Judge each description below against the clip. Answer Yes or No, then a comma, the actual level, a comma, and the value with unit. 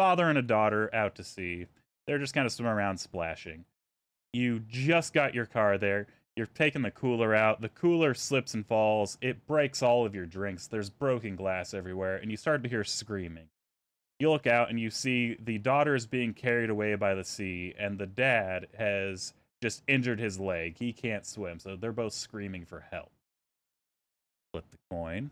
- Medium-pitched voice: No, low, 110 Hz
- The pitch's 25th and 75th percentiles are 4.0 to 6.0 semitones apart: Yes, average, 4.6 semitones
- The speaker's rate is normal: Yes, average, 190 wpm